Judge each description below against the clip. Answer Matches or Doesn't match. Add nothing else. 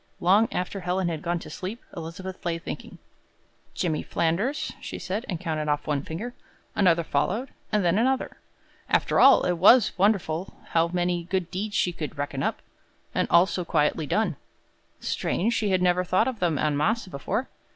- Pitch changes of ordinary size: Matches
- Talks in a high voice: Doesn't match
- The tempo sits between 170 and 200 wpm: Matches